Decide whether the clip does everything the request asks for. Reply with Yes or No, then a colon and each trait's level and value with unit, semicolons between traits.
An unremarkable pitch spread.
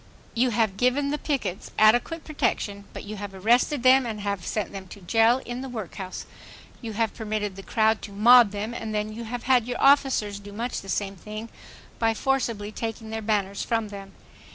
Yes: average, 3.1 semitones